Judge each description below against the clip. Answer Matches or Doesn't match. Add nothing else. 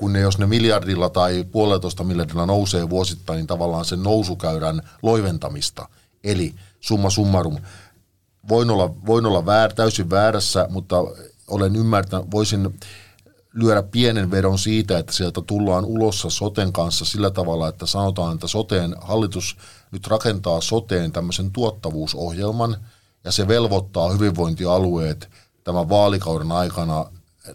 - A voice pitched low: Matches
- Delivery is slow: Doesn't match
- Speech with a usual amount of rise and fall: Matches